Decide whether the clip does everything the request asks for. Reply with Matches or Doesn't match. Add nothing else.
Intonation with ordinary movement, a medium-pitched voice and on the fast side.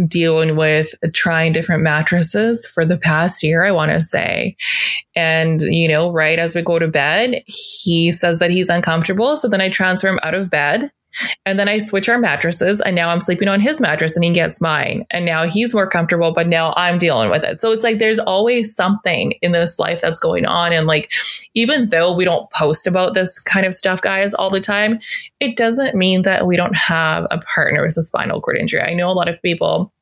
Matches